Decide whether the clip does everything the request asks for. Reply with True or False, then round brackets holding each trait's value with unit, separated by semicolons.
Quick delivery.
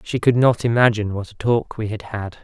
True (245 wpm)